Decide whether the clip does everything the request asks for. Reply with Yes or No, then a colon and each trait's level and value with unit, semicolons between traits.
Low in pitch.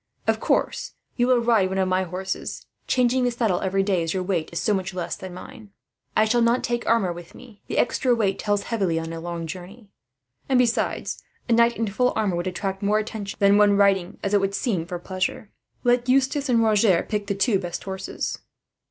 No: high, 200 Hz